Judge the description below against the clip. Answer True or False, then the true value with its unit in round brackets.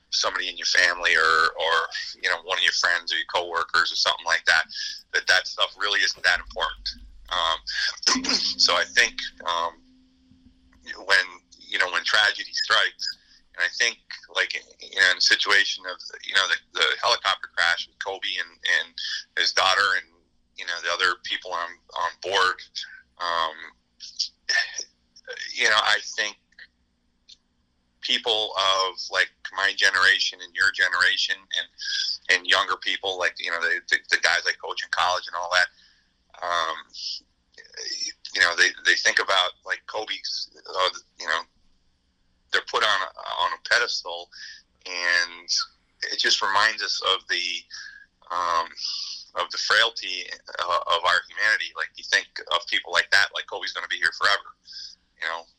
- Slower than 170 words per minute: True (160 wpm)